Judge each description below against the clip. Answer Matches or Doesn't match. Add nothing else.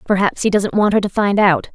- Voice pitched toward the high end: Matches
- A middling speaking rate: Doesn't match